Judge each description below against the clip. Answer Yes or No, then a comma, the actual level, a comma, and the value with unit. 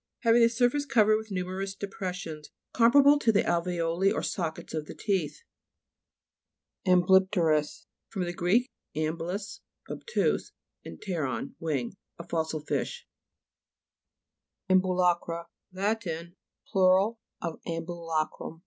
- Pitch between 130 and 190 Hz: Yes, medium, 185 Hz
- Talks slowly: Yes, slow, 115 wpm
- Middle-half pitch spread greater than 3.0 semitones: Yes, average, 3.8 semitones